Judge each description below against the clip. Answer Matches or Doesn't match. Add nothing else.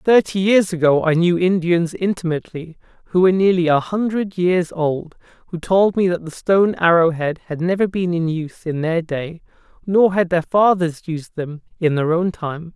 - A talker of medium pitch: Matches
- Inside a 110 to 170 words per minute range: Doesn't match